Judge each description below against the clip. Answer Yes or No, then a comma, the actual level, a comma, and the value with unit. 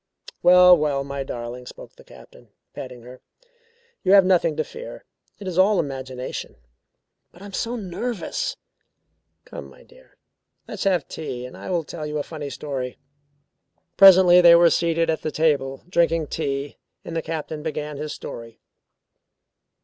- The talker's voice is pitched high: No, medium, 160 Hz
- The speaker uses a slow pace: No, average, 155 wpm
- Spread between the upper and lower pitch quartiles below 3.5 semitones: No, average, 4.6 semitones